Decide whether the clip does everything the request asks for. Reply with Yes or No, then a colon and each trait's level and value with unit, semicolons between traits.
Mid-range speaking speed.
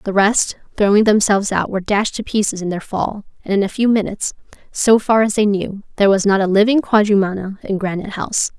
No: fast, 215 wpm